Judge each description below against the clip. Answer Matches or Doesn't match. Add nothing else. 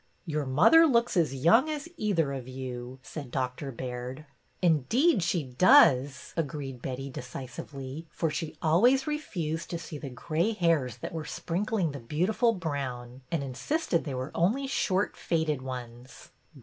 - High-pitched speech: Doesn't match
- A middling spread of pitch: Doesn't match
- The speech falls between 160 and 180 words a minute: Doesn't match